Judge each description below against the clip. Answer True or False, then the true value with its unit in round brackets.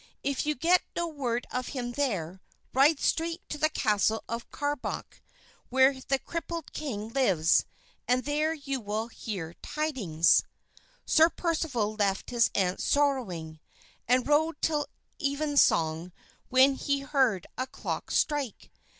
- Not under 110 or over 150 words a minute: True (135 wpm)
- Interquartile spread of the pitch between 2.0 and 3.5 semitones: False (5.5 semitones)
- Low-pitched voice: False (265 Hz)